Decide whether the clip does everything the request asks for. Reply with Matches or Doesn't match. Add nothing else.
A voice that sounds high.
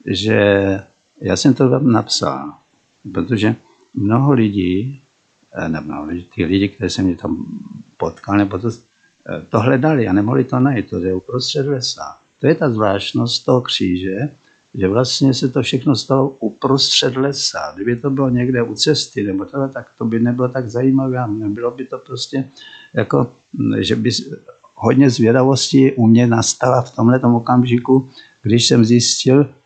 Doesn't match